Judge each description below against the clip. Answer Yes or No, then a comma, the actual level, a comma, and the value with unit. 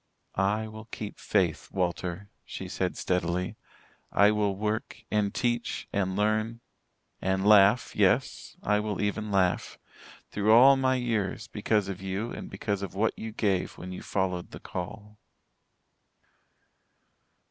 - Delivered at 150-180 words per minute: No, slow, 135 wpm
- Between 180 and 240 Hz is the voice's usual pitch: No, low, 105 Hz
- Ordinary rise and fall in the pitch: No, narrow, 2.3 semitones